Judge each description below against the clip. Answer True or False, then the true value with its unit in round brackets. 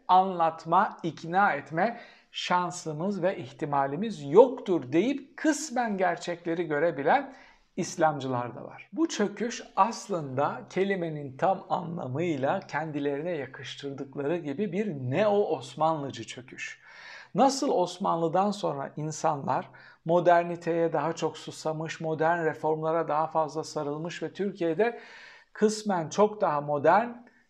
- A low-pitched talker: False (170 Hz)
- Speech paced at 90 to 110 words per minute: True (100 wpm)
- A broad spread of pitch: False (4.2 semitones)